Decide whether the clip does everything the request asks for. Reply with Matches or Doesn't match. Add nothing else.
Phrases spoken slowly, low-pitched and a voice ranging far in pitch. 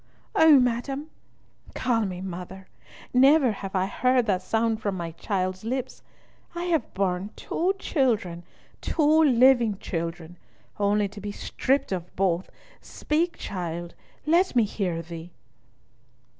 Doesn't match